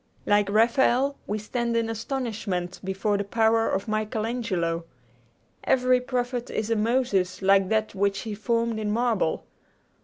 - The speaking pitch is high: Yes, high, 220 Hz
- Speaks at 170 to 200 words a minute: No, average, 145 wpm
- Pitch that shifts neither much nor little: Yes, average, 3.0 semitones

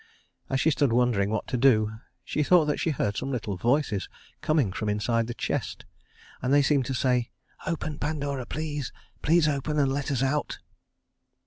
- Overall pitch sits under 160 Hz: Yes, low, 135 Hz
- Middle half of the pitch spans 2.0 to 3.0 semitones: No, average, 3.9 semitones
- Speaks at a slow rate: No, average, 180 wpm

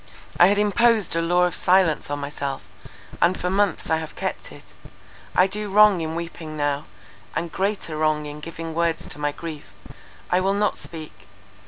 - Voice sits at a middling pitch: Yes, medium, 165 Hz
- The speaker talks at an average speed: Yes, average, 180 wpm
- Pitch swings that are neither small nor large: Yes, average, 3.8 semitones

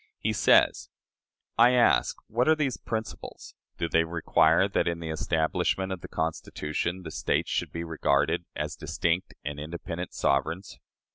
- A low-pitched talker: Yes, very low, 85 Hz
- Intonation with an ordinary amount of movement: Yes, average, 3.1 semitones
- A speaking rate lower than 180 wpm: Yes, average, 150 wpm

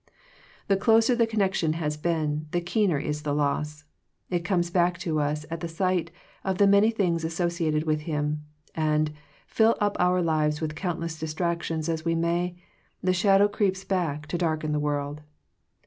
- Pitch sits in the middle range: Yes, medium, 165 Hz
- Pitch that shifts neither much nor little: Yes, average, 3.2 semitones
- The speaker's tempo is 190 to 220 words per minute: No, average, 170 wpm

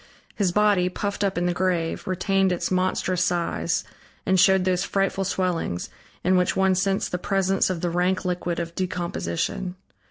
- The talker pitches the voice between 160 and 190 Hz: Yes, medium, 185 Hz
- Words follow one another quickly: No, average, 165 wpm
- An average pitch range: No, narrow, 1.4 semitones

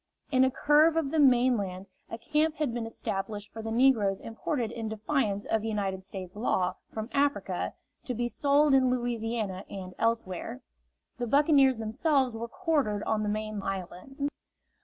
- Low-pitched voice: No, high, 230 Hz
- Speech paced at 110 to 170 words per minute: Yes, average, 160 wpm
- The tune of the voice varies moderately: Yes, average, 4.6 semitones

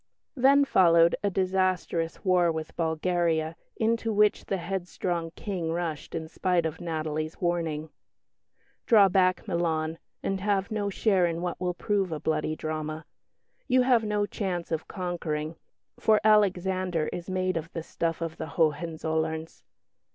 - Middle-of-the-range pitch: Yes, medium, 175 Hz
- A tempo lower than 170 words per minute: Yes, average, 145 wpm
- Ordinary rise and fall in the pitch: Yes, average, 3.0 semitones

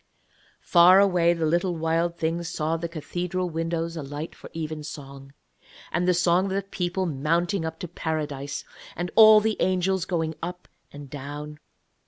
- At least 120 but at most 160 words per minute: Yes, average, 155 wpm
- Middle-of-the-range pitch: Yes, medium, 170 Hz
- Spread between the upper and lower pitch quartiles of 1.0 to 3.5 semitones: Yes, narrow, 2.4 semitones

